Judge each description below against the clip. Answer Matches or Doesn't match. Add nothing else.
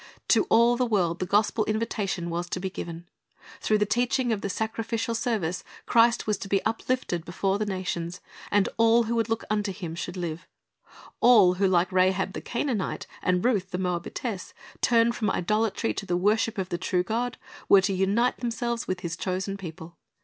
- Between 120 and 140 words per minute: Doesn't match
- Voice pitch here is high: Matches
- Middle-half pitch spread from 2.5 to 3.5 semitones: Doesn't match